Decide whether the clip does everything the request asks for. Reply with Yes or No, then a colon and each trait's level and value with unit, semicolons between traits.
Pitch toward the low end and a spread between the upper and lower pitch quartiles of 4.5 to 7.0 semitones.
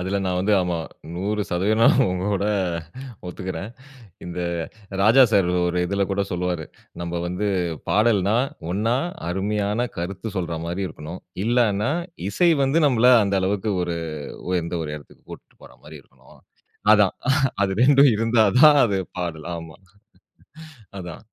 No: very low, 95 Hz; average, 3.4 semitones